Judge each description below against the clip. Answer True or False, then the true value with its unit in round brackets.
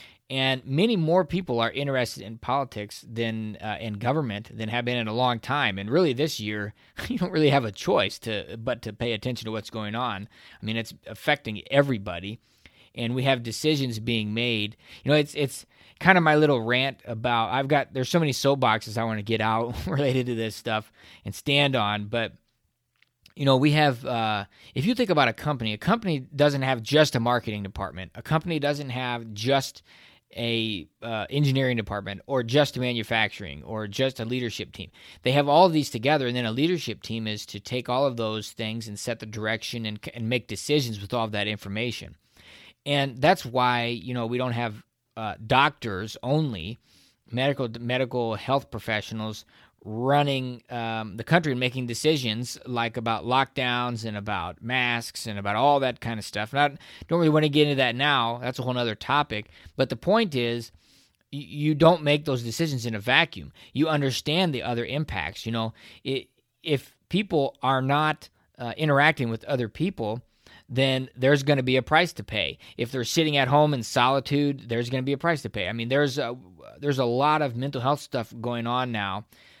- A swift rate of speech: False (195 wpm)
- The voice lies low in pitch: True (125 Hz)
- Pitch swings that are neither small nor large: True (4.0 semitones)